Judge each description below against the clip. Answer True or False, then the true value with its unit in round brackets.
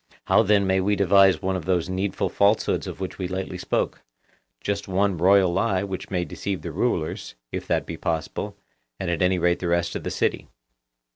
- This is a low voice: True (95 Hz)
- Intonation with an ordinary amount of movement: False (2.1 semitones)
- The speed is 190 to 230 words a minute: True (195 wpm)